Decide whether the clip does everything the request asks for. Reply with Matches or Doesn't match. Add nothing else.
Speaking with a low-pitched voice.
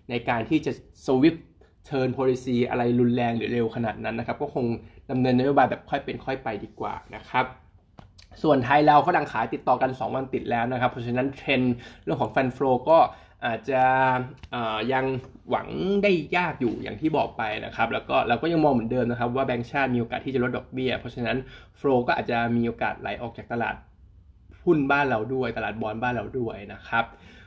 Matches